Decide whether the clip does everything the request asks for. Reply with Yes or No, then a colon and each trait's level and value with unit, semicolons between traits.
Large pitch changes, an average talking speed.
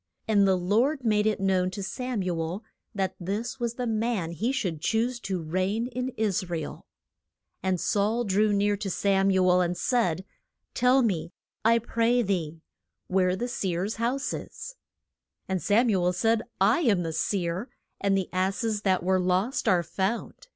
No: average, 3.9 semitones; average, 180 wpm